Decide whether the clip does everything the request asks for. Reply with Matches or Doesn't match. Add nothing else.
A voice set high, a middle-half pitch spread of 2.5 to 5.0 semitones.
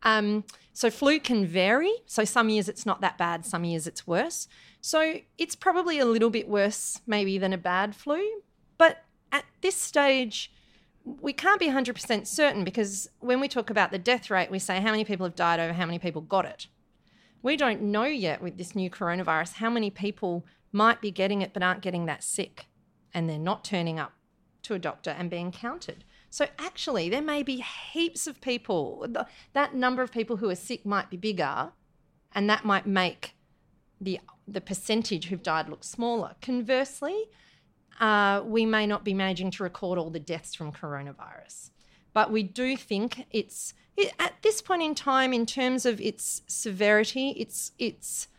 Doesn't match